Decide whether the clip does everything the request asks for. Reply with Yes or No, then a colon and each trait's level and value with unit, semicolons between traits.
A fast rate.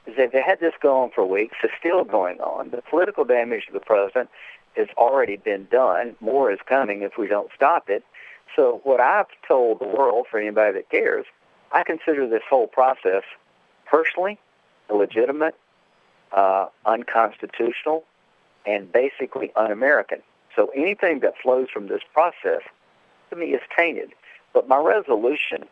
No: average, 150 wpm